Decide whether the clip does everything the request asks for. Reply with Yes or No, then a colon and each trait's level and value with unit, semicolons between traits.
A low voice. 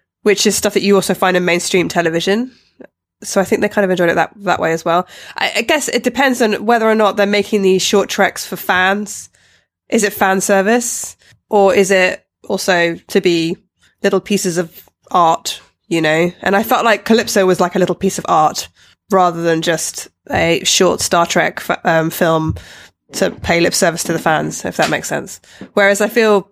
No: high, 195 Hz